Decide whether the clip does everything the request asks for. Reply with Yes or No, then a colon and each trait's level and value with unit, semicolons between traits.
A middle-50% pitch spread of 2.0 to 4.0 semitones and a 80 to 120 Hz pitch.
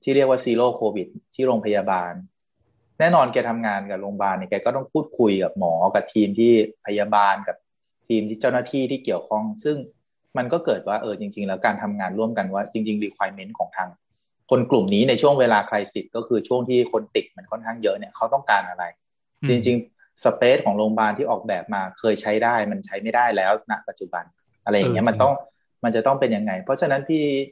Yes: average, 3.5 semitones; low, 110 Hz